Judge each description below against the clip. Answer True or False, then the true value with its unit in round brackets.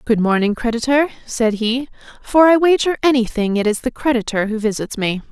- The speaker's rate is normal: True (180 wpm)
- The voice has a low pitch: False (240 Hz)